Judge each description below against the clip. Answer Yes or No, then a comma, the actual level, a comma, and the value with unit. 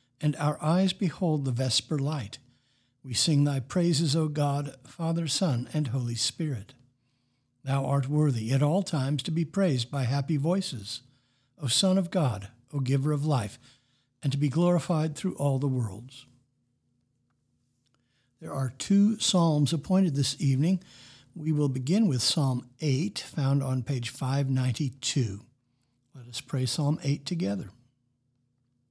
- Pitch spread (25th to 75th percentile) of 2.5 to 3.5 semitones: Yes, average, 3.2 semitones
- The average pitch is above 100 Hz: Yes, low, 135 Hz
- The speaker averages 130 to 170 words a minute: Yes, average, 145 wpm